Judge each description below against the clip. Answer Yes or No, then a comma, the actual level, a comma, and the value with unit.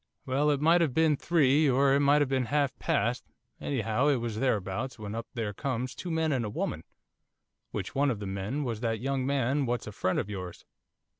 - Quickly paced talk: Yes, fast, 215 wpm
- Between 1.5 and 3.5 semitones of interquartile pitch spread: No, average, 4.1 semitones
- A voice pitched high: No, low, 130 Hz